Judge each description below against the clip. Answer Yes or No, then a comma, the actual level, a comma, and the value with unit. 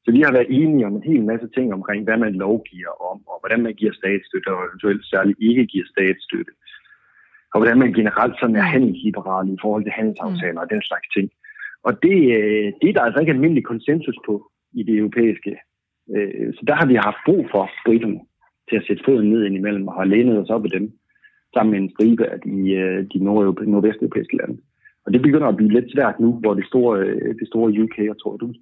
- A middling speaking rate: Yes, average, 215 wpm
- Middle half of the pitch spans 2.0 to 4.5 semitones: Yes, narrow, 2.5 semitones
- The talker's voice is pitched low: Yes, low, 110 Hz